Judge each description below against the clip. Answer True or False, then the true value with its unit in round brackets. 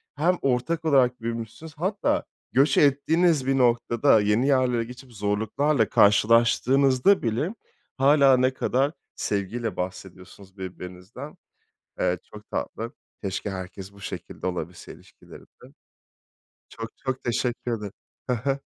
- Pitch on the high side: False (120 Hz)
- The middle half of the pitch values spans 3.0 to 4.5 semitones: False (5.0 semitones)